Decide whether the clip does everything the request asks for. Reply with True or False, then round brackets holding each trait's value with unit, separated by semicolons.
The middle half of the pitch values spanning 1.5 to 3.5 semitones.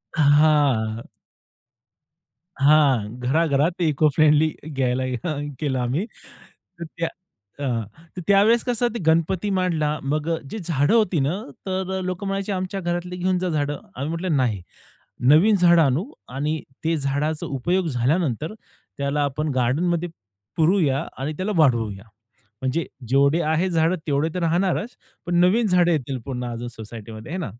False (4.7 semitones)